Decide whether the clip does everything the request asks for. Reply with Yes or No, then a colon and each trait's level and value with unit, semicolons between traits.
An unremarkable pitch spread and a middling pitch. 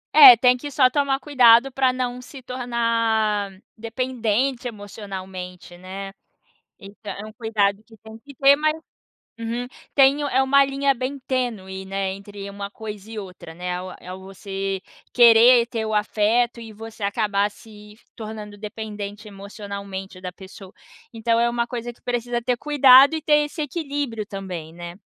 No: average, 4.0 semitones; high, 225 Hz